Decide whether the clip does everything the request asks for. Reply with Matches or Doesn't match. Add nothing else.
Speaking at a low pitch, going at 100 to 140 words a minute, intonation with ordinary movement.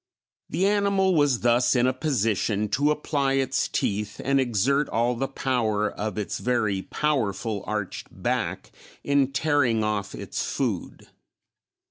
Matches